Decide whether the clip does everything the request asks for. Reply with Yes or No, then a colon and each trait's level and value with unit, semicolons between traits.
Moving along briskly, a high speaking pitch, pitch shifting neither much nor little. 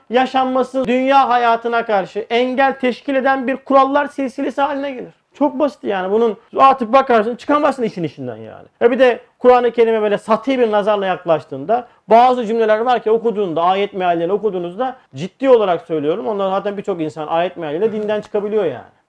Yes: fast, 165 wpm; high, 230 Hz; average, 4.2 semitones